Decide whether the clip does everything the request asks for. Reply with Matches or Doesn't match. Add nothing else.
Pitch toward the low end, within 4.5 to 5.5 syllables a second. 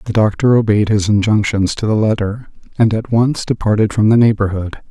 Matches